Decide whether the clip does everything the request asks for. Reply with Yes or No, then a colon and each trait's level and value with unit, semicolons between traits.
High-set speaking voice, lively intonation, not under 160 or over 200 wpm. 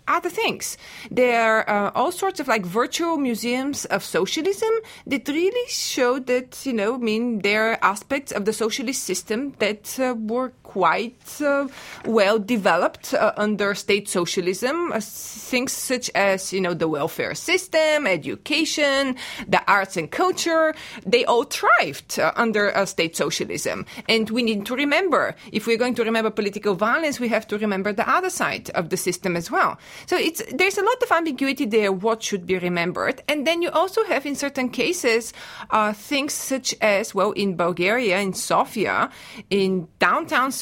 Yes: high, 240 Hz; wide, 5.8 semitones; average, 170 wpm